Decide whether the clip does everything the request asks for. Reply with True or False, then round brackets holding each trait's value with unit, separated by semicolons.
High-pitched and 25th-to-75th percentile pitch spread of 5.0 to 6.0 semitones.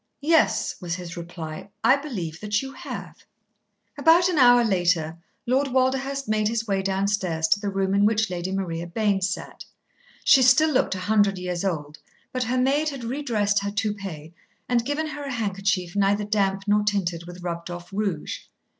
True (205 Hz; 5.5 semitones)